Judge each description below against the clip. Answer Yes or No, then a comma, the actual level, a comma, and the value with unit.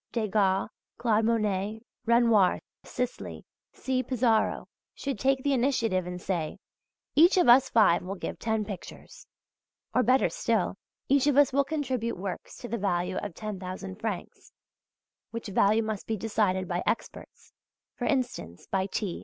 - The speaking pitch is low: No, high, 220 Hz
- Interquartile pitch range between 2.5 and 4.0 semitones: No, average, 4.7 semitones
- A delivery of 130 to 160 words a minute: Yes, average, 145 wpm